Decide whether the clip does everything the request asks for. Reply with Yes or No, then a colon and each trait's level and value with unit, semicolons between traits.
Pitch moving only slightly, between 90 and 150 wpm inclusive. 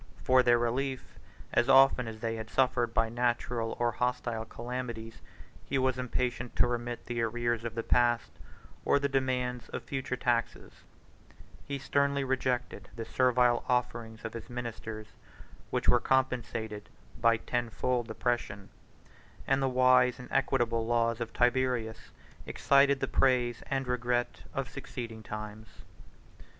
Yes: narrow, 1.8 semitones; average, 140 wpm